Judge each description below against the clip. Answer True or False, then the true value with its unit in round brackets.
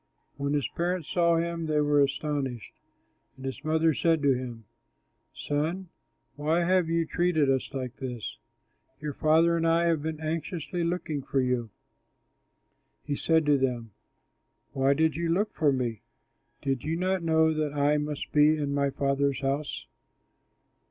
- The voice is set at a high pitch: False (150 Hz)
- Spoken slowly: False (155 wpm)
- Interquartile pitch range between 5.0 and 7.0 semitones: False (3.1 semitones)